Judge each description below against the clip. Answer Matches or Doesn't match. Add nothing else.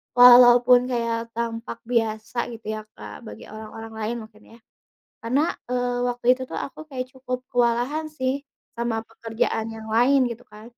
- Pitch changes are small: Matches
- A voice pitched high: Matches